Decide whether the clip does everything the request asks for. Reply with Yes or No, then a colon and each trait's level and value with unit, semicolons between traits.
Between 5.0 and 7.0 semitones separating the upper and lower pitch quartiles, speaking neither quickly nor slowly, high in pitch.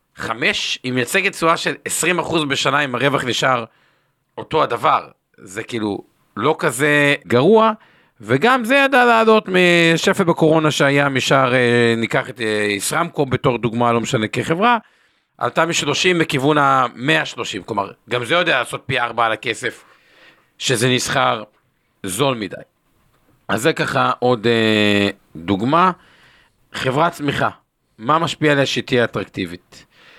No: wide, 5.6 semitones; average, 125 wpm; medium, 140 Hz